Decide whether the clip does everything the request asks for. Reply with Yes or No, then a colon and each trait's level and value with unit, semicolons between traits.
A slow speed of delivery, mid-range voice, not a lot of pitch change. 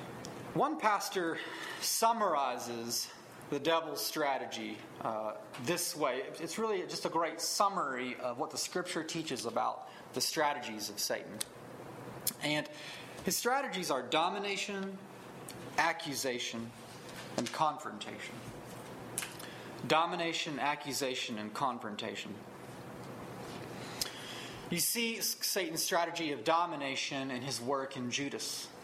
No: slow, 100 wpm; medium, 150 Hz; wide, 5.5 semitones